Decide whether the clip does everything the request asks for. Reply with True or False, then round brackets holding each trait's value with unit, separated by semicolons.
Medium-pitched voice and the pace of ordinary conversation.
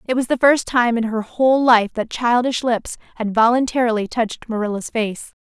False (235 Hz; 190 wpm)